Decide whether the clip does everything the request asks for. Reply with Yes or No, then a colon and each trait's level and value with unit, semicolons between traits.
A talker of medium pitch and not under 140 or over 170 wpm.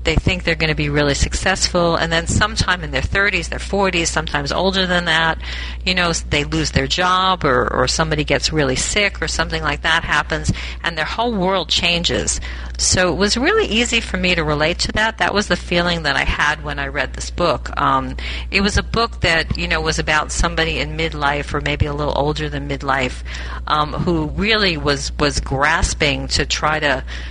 No: medium, 160 Hz; fast, 205 wpm